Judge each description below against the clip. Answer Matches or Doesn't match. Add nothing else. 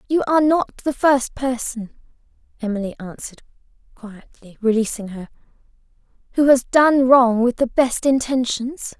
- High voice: Matches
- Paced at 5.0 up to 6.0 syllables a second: Doesn't match